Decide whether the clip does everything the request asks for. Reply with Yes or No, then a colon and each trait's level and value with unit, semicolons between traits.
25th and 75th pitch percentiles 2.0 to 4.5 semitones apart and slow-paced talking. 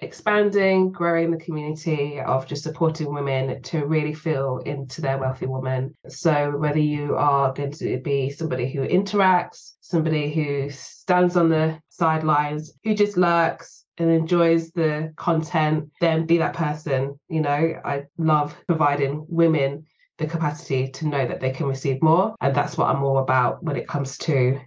No: average, 3.0 semitones; average, 165 wpm